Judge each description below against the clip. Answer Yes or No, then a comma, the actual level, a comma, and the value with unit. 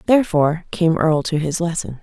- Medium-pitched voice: Yes, medium, 165 Hz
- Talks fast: No, average, 180 wpm